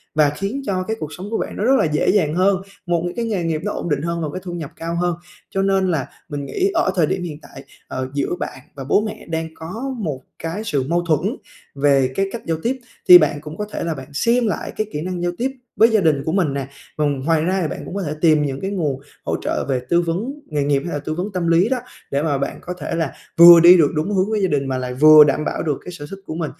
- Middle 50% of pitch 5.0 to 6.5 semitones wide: No, average, 4.5 semitones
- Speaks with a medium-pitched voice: Yes, medium, 165 Hz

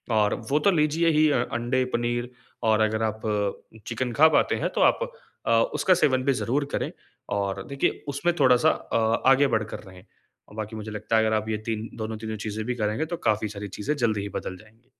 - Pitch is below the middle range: Yes, low, 110 Hz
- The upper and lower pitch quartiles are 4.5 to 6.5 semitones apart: No, average, 3.3 semitones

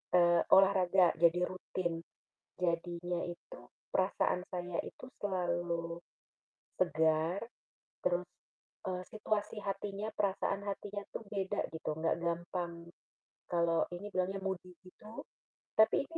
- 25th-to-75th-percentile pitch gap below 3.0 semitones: Yes, narrow, 2.5 semitones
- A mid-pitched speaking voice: Yes, medium, 180 Hz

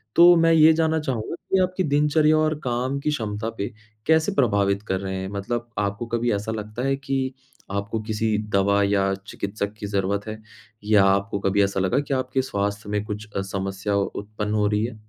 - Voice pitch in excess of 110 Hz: No, low, 105 Hz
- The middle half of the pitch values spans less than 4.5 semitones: No, average, 5.1 semitones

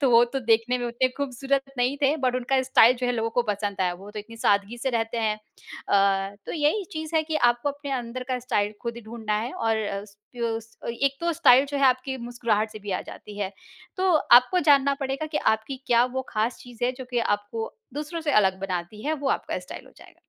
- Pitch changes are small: No, average, 4.1 semitones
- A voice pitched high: Yes, high, 240 Hz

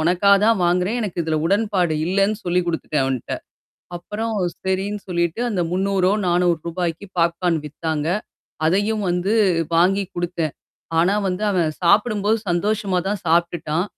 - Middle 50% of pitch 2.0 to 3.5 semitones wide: Yes, average, 2.9 semitones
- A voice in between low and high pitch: Yes, medium, 180 Hz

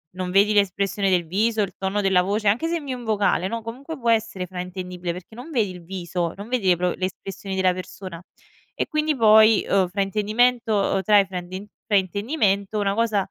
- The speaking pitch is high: Yes, high, 200 Hz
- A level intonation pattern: No, average, 3.2 semitones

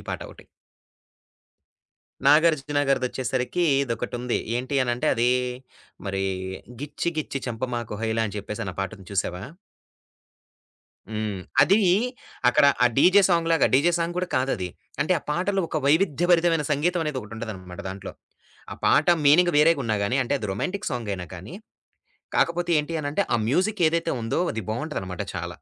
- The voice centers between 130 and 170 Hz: Yes, low, 135 Hz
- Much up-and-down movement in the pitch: Yes, wide, 7.1 semitones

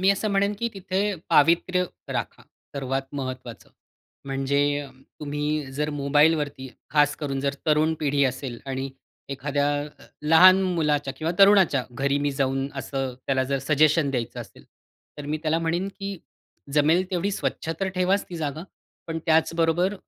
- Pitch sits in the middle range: Yes, medium, 150 Hz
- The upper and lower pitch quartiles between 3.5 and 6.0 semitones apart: Yes, average, 3.8 semitones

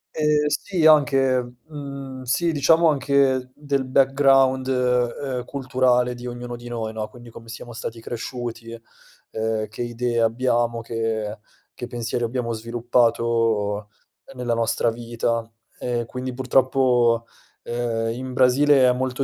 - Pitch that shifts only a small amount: Yes, narrow, 2.3 semitones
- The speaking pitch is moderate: No, low, 125 Hz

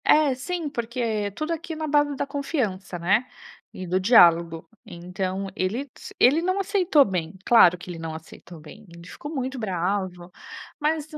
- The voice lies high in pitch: Yes, high, 220 Hz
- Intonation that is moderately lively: No, wide, 8.4 semitones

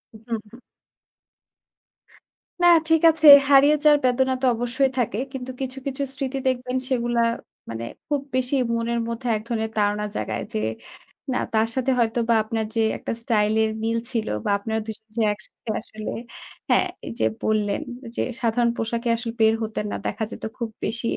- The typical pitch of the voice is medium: No, high, 235 Hz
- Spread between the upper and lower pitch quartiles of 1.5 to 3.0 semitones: Yes, average, 2.7 semitones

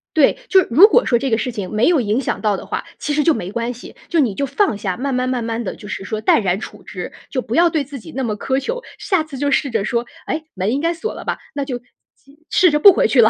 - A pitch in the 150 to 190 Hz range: No, very high, 260 Hz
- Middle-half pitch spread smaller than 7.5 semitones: Yes, average, 5.3 semitones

